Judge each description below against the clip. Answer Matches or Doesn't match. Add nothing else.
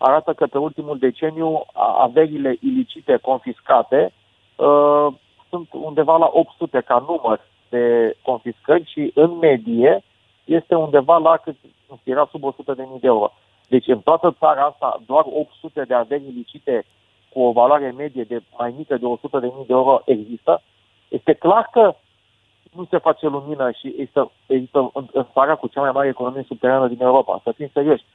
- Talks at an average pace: Matches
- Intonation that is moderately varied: Matches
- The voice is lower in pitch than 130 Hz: Doesn't match